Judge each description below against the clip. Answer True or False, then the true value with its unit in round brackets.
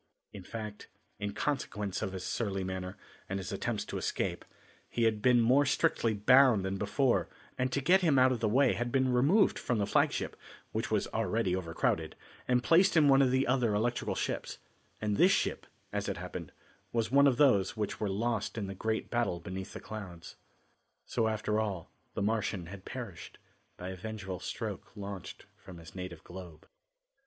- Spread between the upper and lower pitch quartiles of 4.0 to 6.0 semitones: True (4.7 semitones)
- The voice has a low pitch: True (110 Hz)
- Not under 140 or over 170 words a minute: False (185 wpm)